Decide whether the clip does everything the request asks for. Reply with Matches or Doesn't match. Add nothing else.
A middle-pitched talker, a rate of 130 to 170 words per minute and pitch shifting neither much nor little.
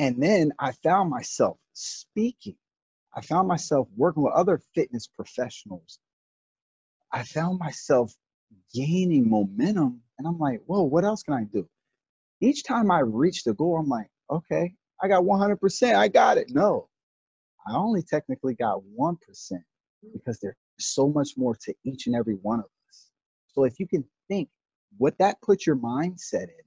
Doesn't match